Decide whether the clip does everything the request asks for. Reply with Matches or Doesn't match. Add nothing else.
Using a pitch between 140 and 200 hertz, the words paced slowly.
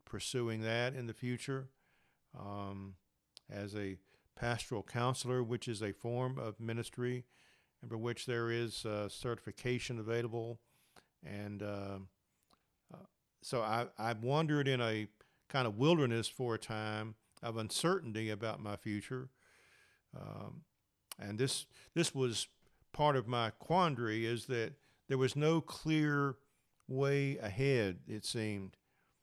Doesn't match